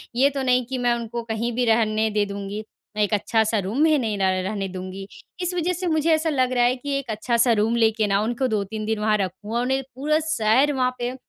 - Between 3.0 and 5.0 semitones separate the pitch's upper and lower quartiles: Yes, average, 3.6 semitones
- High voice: Yes, high, 235 Hz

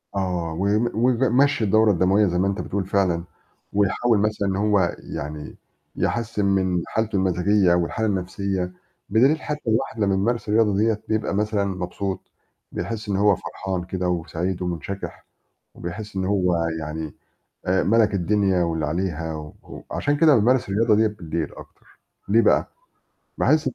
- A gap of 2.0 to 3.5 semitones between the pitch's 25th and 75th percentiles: Yes, average, 3.2 semitones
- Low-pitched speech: Yes, low, 100 Hz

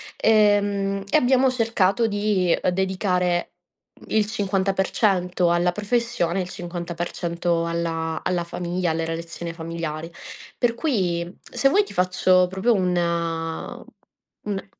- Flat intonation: No, average, 3.2 semitones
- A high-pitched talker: No, medium, 180 Hz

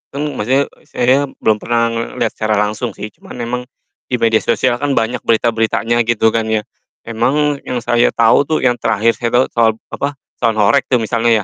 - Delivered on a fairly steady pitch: Yes, narrow, 2.0 semitones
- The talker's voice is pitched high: No, low, 115 Hz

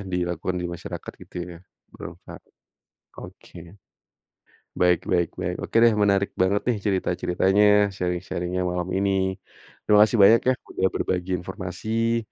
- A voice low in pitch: Yes, very low, 95 Hz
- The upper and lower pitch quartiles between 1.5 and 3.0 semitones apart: Yes, narrow, 2.5 semitones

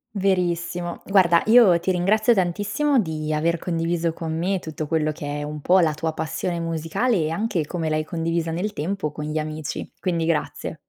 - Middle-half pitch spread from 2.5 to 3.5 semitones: Yes, average, 2.8 semitones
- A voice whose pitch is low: No, medium, 170 Hz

